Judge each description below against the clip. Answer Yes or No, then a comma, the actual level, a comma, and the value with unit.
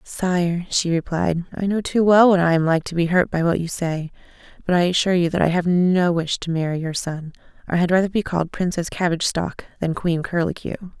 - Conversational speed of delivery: No, fast, 230 wpm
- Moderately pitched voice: Yes, medium, 175 Hz